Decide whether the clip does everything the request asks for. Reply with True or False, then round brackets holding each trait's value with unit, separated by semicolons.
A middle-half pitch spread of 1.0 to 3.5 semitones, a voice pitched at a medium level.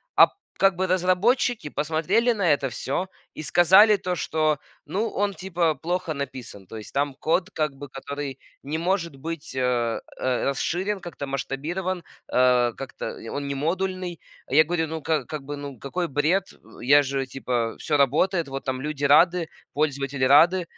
False (4.7 semitones; 155 Hz)